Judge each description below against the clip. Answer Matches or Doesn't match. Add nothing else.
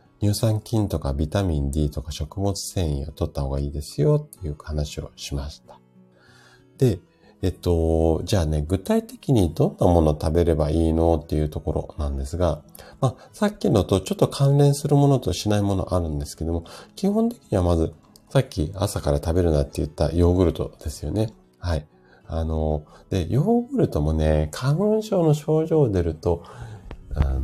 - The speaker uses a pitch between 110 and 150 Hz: Doesn't match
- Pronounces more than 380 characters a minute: Doesn't match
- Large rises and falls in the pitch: Matches